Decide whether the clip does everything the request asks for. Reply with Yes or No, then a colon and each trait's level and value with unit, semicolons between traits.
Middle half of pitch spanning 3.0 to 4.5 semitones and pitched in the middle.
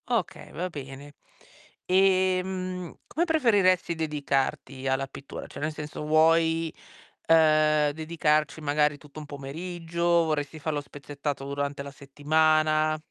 No: narrow, 2.6 semitones; medium, 155 Hz